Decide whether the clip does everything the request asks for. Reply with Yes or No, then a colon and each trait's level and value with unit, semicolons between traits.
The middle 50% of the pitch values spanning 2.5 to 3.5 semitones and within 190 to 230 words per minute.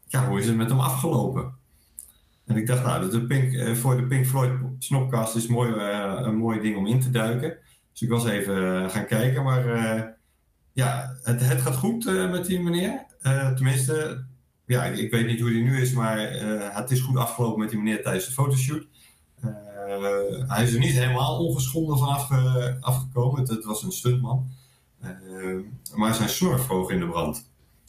Yes: average, 3.2 semitones; fast, 200 wpm